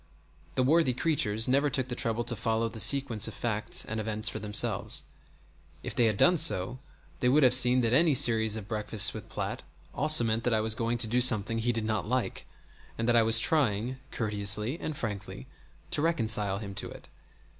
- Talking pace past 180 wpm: Yes, average, 200 wpm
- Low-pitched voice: Yes, low, 115 Hz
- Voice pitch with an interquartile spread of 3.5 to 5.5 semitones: No, average, 2.8 semitones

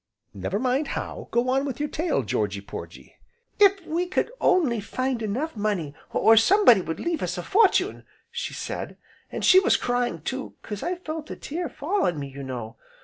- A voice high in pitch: Yes, very high, 255 Hz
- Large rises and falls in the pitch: Yes, wide, 8.7 semitones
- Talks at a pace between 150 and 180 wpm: No, average, 190 wpm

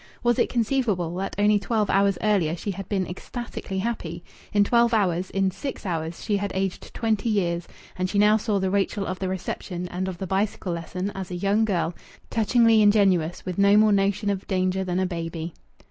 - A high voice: Yes, high, 195 Hz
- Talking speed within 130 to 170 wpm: No, average, 200 wpm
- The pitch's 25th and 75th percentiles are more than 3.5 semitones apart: No, narrow, 2.6 semitones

